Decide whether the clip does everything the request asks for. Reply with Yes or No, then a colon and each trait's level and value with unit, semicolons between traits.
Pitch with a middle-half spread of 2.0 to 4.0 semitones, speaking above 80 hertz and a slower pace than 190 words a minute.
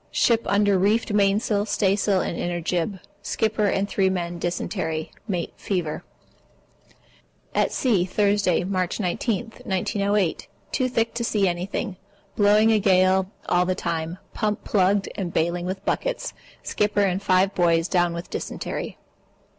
Yes: average, 2.8 semitones; high, 190 Hz; average, 140 wpm